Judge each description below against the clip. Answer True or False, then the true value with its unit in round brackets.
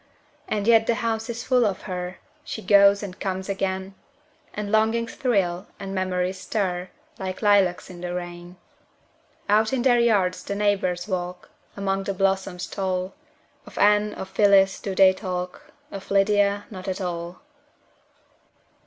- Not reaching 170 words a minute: True (150 wpm)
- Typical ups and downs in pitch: False (2.1 semitones)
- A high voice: True (195 Hz)